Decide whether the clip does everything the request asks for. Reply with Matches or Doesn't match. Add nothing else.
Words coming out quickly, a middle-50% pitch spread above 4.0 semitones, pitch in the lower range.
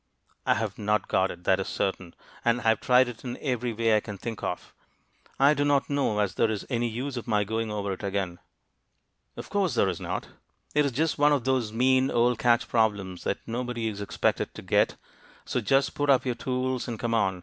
Doesn't match